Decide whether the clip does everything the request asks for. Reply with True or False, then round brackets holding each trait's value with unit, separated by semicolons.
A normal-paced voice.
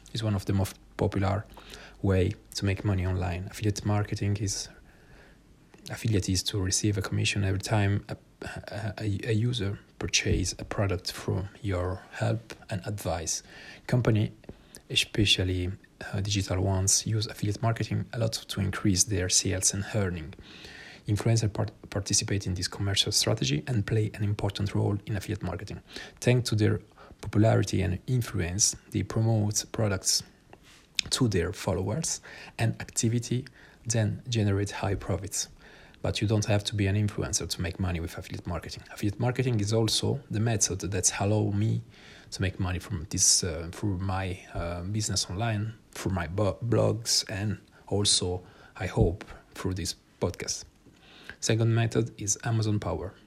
True (150 wpm)